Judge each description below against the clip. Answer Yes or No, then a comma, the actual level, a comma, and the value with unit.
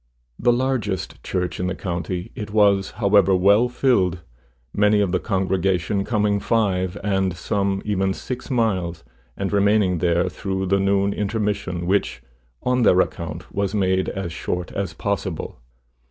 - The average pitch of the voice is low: Yes, very low, 95 Hz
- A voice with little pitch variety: Yes, narrow, 2.1 semitones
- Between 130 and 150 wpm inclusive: Yes, average, 145 wpm